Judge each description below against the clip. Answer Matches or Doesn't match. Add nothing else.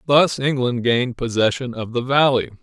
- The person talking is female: Doesn't match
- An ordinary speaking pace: Matches